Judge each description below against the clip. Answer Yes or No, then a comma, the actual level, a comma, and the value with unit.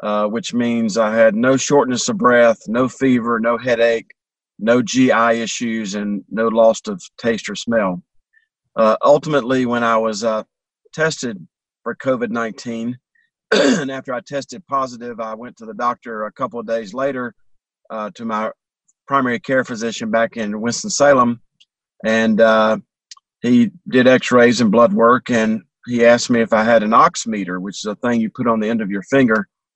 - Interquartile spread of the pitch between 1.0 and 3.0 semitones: Yes, average, 2.7 semitones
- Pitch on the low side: Yes, low, 120 Hz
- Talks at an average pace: Yes, average, 170 wpm